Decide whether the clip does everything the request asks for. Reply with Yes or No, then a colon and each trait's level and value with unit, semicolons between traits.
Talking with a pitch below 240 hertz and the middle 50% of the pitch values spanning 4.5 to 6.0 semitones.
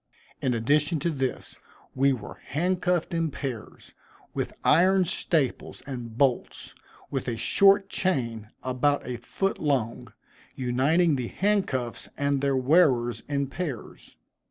Yes: medium, 140 Hz; average, 5.2 semitones